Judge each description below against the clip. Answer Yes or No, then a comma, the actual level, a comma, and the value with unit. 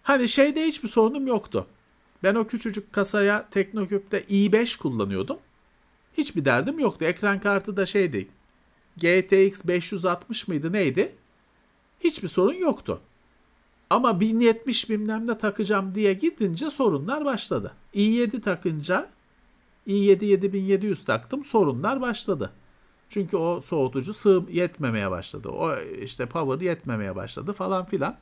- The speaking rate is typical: Yes, average, 115 wpm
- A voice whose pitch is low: No, high, 200 Hz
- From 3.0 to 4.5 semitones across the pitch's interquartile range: Yes, average, 3.9 semitones